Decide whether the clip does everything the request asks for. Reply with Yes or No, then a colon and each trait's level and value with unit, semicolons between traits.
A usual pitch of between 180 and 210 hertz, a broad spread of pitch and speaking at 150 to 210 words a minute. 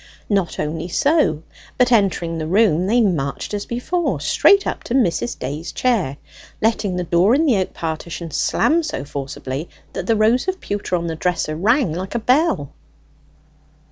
Yes: high, 190 Hz; wide, 6.7 semitones; average, 170 wpm